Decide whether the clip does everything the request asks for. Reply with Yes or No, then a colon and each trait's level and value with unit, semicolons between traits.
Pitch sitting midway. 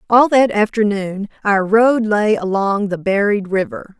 No: high, 205 Hz